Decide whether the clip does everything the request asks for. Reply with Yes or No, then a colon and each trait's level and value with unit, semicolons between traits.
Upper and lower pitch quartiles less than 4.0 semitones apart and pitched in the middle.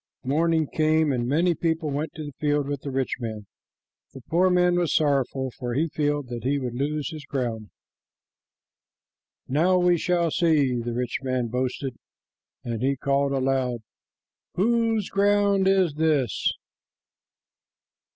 No: average, 4.4 semitones; medium, 145 Hz